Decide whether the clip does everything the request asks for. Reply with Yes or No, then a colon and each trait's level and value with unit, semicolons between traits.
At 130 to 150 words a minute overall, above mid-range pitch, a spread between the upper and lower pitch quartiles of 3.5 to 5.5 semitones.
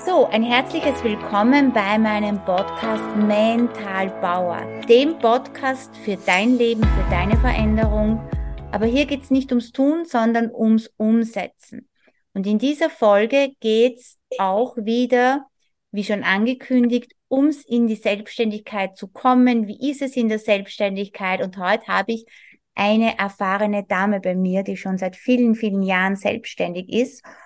Yes: average, 145 wpm; high, 220 Hz; average, 4.2 semitones